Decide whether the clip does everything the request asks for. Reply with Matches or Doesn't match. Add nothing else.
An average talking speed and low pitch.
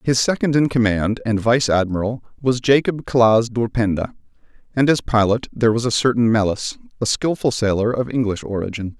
Matches